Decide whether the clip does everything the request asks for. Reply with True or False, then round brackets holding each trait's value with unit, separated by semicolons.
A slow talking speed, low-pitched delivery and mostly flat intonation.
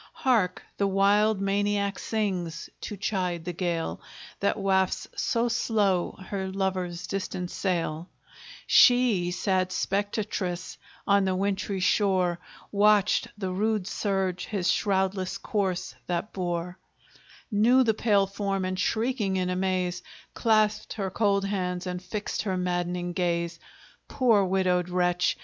False (125 wpm; 190 Hz; 2.2 semitones)